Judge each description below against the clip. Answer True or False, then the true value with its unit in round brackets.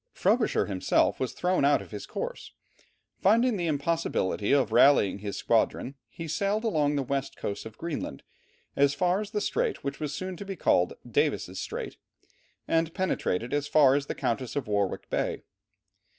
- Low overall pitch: False (145 Hz)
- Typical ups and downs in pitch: False (6.2 semitones)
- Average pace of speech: True (170 wpm)